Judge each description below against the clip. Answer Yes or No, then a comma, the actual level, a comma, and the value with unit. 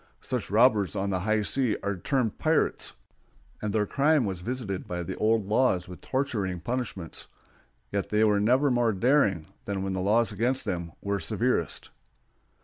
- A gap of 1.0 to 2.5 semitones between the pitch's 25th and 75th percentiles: No, average, 4.4 semitones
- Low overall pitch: Yes, low, 105 Hz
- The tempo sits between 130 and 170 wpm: Yes, average, 165 wpm